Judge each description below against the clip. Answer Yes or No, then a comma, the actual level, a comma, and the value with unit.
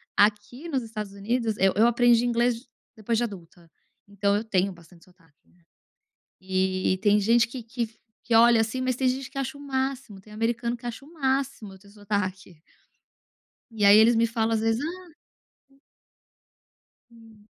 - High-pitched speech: Yes, high, 225 Hz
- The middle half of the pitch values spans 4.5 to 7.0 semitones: No, average, 3.3 semitones